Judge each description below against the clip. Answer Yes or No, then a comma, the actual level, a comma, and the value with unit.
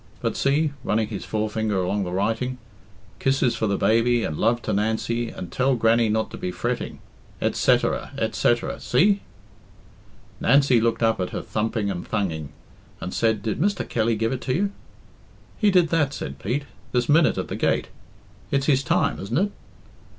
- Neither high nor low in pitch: No, low, 115 Hz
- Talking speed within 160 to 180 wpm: Yes, average, 175 wpm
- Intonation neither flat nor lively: Yes, average, 4.2 semitones